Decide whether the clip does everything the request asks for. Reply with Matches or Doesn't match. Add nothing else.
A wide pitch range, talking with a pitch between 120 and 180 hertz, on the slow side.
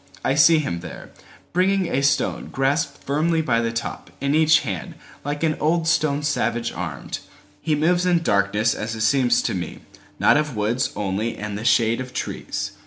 Doesn't match